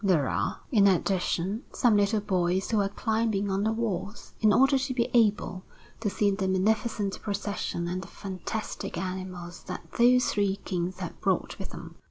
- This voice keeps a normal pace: Yes, average, 175 wpm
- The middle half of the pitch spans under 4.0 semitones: Yes, average, 2.9 semitones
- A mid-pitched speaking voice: No, high, 200 Hz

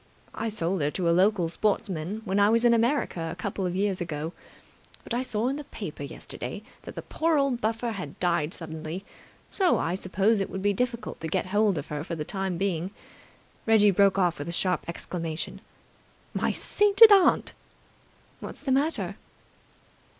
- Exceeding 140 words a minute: Yes, average, 180 wpm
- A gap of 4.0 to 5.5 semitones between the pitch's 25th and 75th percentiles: Yes, average, 5.1 semitones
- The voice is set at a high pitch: Yes, high, 195 Hz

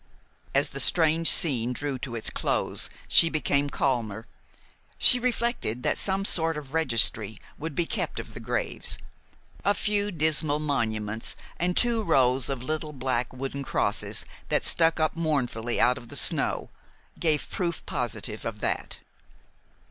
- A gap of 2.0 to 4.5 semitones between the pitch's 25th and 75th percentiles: No, average, 5.1 semitones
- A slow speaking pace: No, average, 150 wpm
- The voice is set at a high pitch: No, medium, 145 Hz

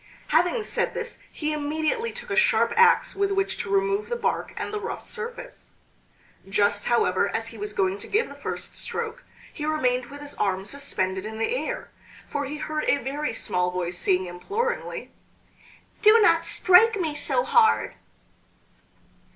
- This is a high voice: Yes, very high, 300 Hz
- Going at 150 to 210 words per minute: Yes, average, 165 wpm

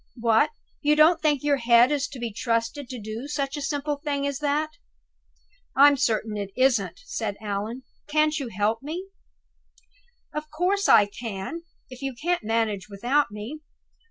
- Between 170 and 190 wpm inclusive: No, average, 160 wpm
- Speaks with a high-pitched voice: Yes, very high, 270 Hz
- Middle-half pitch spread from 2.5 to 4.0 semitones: No, average, 5.0 semitones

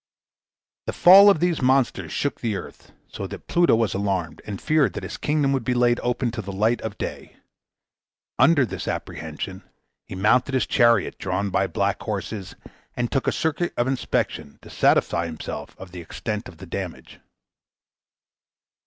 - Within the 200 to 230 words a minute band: No, average, 170 wpm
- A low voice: Yes, low, 120 Hz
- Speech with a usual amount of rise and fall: No, wide, 5.7 semitones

